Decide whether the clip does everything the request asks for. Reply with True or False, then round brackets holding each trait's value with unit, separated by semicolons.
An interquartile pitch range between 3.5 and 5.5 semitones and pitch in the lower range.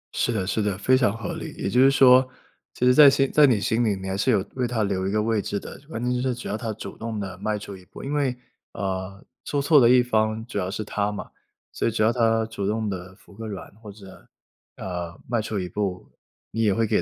True (3.8 semitones; 110 Hz)